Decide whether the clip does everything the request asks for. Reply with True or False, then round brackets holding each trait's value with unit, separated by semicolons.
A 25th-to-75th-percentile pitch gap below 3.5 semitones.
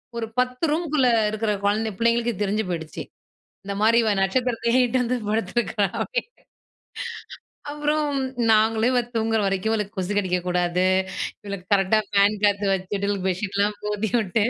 True (2.9 semitones)